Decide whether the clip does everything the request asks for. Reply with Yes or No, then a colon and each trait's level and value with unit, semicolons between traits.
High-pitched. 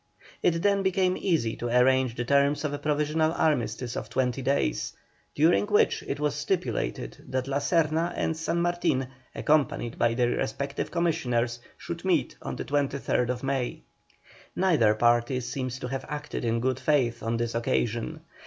No: low, 135 Hz